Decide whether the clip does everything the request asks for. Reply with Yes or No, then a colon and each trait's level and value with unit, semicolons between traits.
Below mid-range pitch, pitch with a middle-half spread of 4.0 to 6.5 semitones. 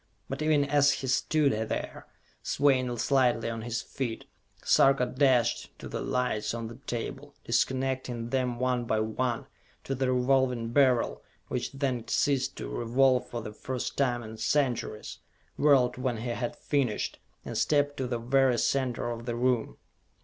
No: low, 125 Hz; narrow, 2.4 semitones